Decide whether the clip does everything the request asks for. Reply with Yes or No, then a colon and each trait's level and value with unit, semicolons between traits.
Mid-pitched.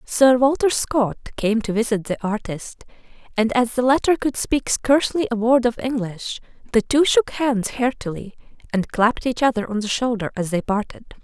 No: high, 235 Hz